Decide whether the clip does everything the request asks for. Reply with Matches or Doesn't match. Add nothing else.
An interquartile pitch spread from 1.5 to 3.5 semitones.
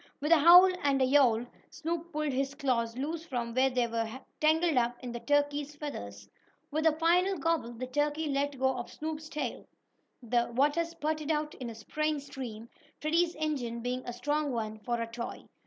Doesn't match